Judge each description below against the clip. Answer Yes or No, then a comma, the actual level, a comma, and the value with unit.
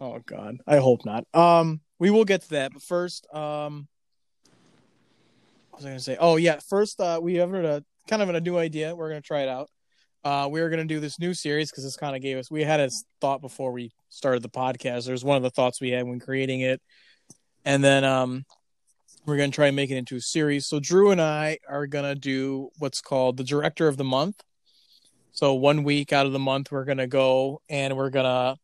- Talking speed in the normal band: No, fast, 225 wpm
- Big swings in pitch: No, average, 2.8 semitones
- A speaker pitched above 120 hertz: Yes, medium, 140 Hz